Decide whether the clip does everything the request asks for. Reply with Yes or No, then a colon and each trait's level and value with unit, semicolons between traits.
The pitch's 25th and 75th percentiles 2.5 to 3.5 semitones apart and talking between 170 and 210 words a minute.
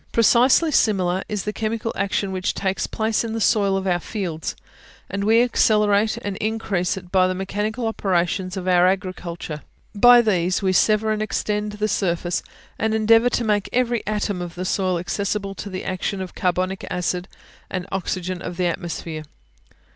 Yes: average, 2.9 semitones; average, 175 wpm